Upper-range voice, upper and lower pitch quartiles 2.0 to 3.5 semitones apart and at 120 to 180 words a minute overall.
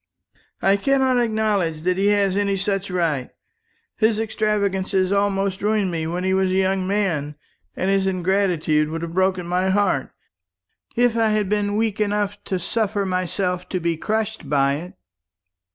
Yes: high, 195 Hz; narrow, 2.4 semitones; average, 160 wpm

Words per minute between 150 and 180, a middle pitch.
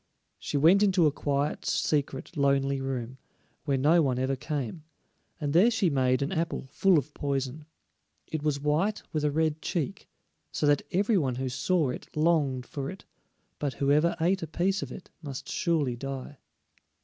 Yes: average, 175 wpm; medium, 145 Hz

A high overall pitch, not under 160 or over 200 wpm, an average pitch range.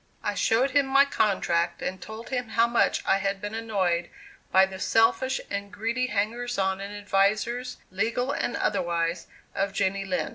Yes: high, 205 Hz; average, 170 wpm; average, 3.5 semitones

